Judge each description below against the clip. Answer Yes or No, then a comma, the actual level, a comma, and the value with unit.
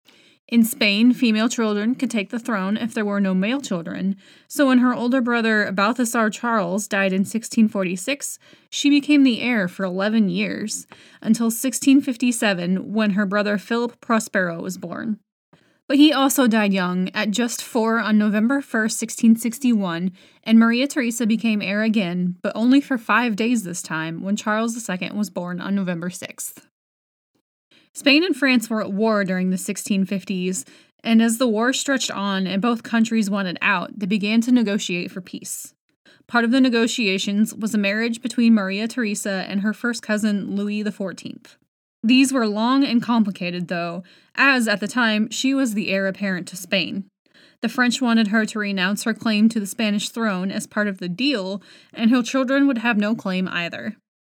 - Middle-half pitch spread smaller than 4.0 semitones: Yes, average, 3.3 semitones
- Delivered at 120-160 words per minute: No, average, 175 wpm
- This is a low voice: No, high, 220 Hz